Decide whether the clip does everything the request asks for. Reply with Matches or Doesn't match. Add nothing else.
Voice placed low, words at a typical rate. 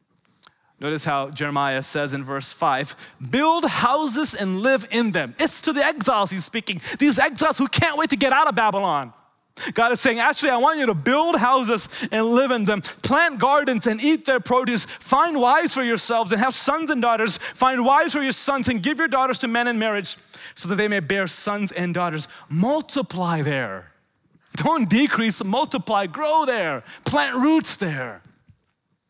Doesn't match